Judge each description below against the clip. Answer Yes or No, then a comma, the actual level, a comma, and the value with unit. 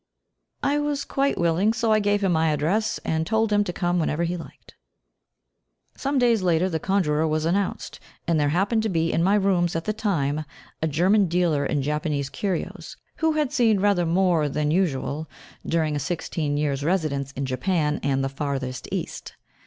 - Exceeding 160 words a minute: Yes, average, 185 wpm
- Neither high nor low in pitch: Yes, medium, 170 Hz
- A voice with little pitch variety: No, average, 5.1 semitones